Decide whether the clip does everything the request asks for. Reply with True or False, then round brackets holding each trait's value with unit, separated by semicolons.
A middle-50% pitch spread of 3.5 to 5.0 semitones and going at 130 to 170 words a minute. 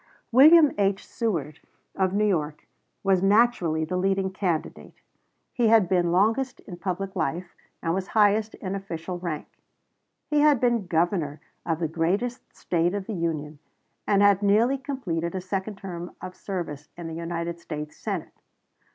True (3.8 semitones; 155 wpm)